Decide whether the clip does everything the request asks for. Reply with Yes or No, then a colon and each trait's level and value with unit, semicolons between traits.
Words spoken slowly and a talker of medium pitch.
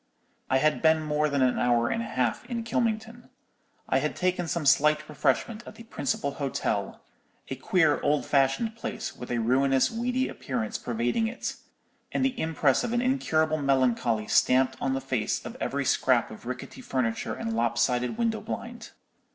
No: average, 165 wpm; medium, 145 Hz